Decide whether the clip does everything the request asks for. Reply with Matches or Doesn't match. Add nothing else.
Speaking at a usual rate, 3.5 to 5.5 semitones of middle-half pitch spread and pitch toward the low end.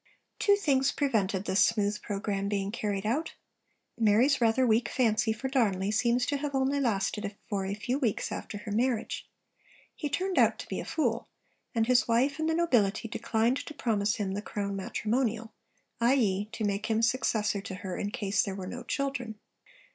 Doesn't match